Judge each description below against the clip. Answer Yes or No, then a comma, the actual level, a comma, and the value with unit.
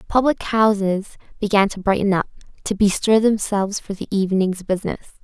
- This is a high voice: Yes, high, 200 Hz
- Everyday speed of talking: Yes, average, 150 wpm